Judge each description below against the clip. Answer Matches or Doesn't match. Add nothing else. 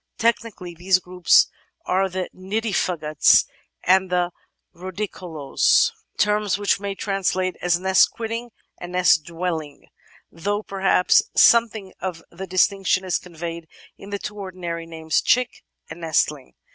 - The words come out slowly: Matches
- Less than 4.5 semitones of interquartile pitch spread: Matches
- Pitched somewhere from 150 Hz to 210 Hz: Matches